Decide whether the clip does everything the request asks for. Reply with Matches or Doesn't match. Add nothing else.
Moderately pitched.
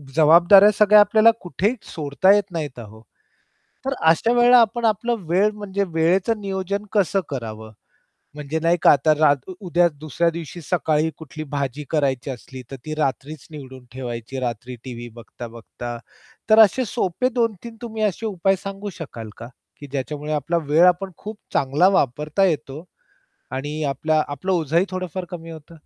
Matches